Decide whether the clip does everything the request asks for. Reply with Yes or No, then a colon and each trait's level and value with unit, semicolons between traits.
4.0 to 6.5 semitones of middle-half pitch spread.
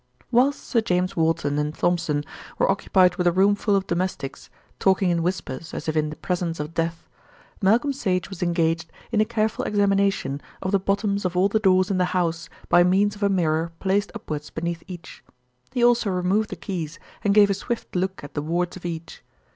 No: average, 3.2 semitones